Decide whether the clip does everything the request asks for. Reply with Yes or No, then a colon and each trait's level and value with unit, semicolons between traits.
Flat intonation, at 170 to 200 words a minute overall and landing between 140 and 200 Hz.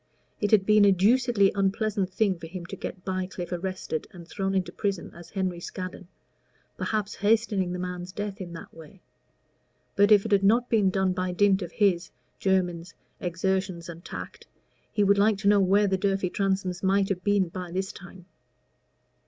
Yes: narrow, 1.9 semitones; average, 180 wpm; high, 190 Hz